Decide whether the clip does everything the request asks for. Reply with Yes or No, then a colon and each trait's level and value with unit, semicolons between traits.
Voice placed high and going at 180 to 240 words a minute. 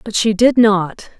Yes: high, 210 Hz; average, 200 wpm